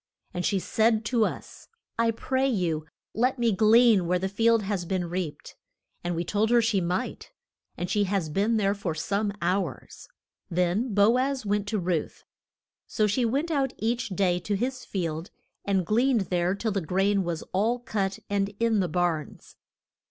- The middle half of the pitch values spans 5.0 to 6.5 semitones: No, average, 4.1 semitones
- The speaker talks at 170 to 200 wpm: Yes, average, 175 wpm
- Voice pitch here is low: No, high, 200 Hz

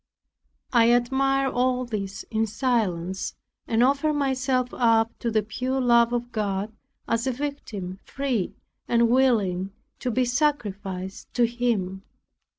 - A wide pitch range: No, average, 3.6 semitones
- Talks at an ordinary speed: No, slow, 130 wpm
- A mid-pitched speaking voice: No, high, 235 Hz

